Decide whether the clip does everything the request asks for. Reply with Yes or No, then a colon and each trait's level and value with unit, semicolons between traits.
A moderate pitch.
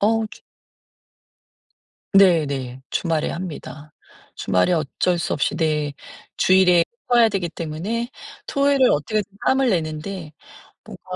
Yes: medium, 175 Hz